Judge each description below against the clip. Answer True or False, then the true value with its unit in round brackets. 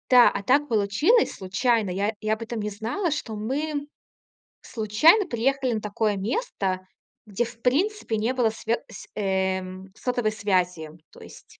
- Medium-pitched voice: False (225 Hz)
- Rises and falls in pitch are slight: False (4.1 semitones)